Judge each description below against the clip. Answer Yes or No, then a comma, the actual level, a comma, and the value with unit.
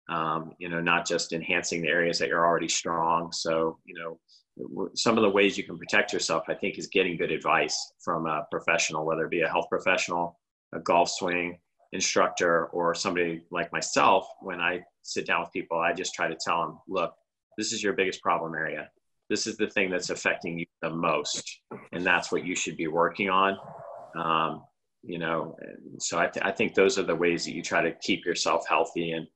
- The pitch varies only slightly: Yes, narrow, 2.3 semitones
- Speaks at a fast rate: Yes, fast, 210 wpm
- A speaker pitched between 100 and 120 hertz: No, very low, 85 Hz